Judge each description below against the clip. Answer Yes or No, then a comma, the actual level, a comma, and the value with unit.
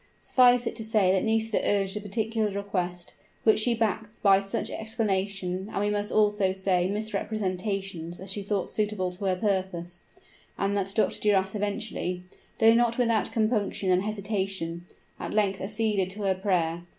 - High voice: Yes, high, 200 Hz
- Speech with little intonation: Yes, narrow, 2.3 semitones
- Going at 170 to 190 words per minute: No, average, 160 wpm